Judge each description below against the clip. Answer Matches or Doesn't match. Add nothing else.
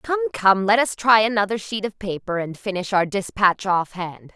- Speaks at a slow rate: Doesn't match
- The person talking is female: Matches